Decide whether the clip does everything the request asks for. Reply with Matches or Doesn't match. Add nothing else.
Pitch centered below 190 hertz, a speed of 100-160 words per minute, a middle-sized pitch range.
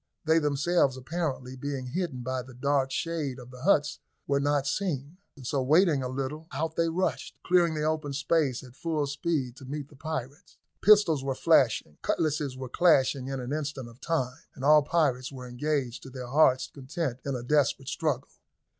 Doesn't match